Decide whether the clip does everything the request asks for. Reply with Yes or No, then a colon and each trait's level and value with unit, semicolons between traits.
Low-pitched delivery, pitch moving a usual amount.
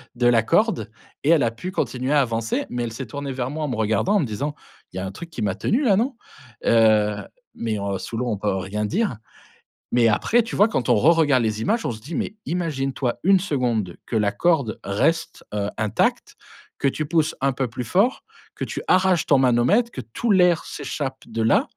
No: low, 130 Hz; wide, 7.0 semitones